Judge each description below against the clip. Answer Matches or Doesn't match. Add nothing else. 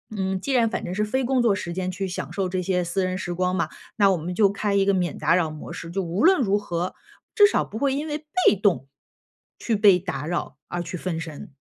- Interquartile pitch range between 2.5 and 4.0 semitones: Matches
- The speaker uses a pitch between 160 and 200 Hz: Matches